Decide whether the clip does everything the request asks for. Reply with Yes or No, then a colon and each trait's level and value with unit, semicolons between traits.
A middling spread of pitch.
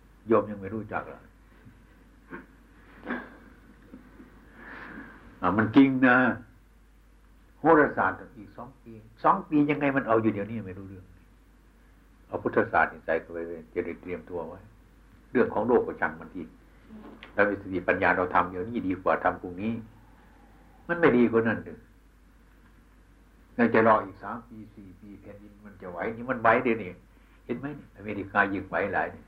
Yes: average, 3.4 semitones